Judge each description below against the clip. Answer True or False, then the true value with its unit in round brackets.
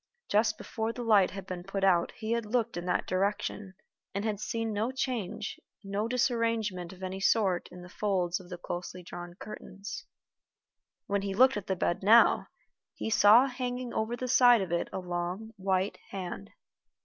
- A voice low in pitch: False (200 Hz)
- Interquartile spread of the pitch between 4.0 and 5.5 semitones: False (3.6 semitones)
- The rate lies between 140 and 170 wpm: False (180 wpm)